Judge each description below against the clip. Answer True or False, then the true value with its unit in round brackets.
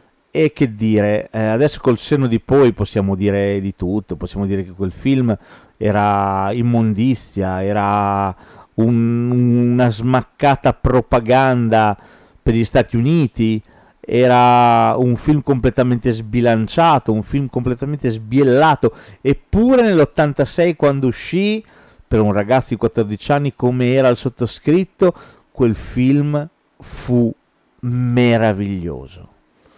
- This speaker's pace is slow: True (110 wpm)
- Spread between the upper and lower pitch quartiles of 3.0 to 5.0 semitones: True (3.9 semitones)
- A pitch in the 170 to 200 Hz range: False (120 Hz)